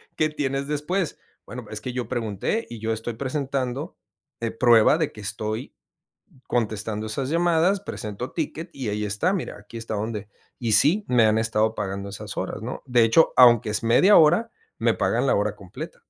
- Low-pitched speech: Yes, low, 120 Hz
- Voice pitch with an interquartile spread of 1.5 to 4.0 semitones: No, wide, 5.5 semitones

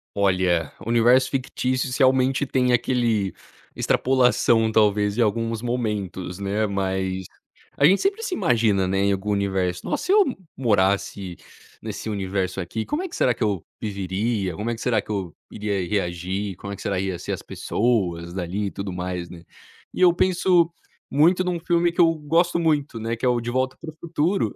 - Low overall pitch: Yes, low, 110 Hz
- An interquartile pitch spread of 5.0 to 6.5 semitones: Yes, wide, 5.4 semitones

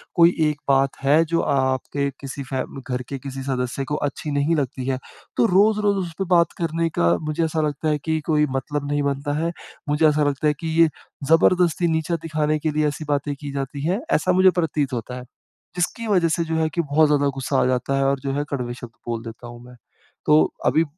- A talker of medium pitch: Yes, medium, 145 Hz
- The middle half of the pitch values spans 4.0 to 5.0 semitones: No, average, 3.1 semitones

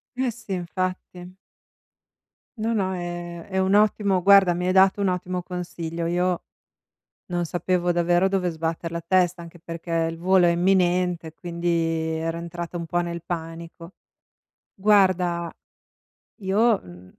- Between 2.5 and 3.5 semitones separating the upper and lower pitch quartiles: No, narrow, 1.8 semitones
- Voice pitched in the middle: Yes, medium, 175 Hz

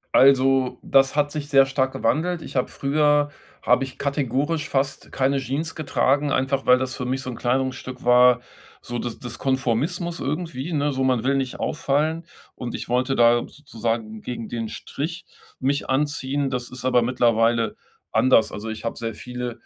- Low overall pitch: Yes, low, 130 Hz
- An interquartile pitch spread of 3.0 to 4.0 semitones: No, narrow, 2.6 semitones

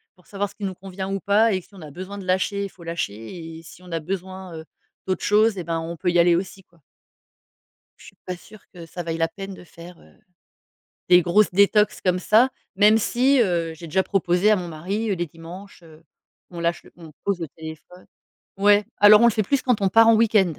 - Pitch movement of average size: Yes, average, 3.2 semitones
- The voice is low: No, medium, 185 Hz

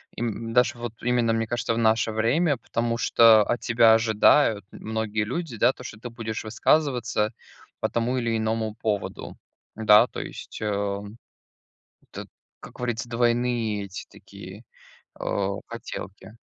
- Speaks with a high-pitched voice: No, low, 115 Hz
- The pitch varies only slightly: Yes, narrow, 1.8 semitones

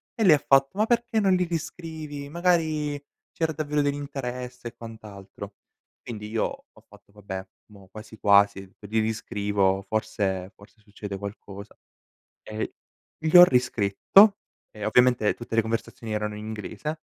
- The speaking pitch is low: Yes, low, 115 Hz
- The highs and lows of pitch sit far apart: Yes, wide, 6.5 semitones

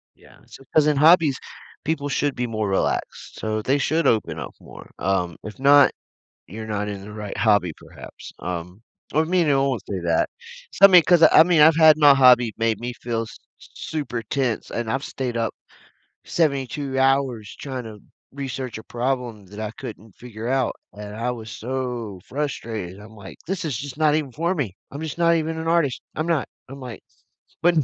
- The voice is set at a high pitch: No, low, 125 Hz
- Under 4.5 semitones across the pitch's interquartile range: No, average, 5.3 semitones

